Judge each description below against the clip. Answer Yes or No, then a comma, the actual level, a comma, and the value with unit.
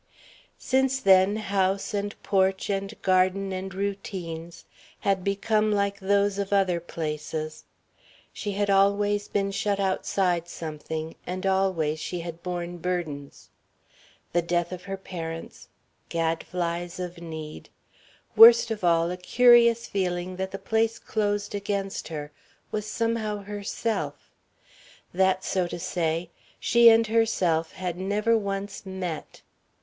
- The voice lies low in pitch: No, high, 190 Hz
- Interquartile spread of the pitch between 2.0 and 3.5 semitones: Yes, average, 2.8 semitones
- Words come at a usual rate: No, slow, 125 wpm